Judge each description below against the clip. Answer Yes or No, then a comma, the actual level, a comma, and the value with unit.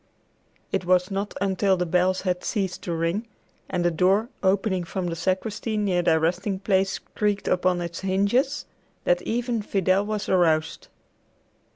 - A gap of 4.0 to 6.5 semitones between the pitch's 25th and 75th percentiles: No, narrow, 2.4 semitones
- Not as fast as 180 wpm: Yes, average, 155 wpm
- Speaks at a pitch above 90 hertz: Yes, high, 190 Hz